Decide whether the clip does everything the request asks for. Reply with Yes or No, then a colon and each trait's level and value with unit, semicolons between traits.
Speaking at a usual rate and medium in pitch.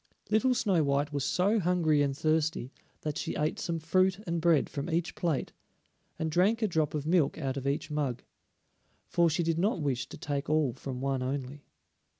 Yes: average, 190 wpm; medium, 155 Hz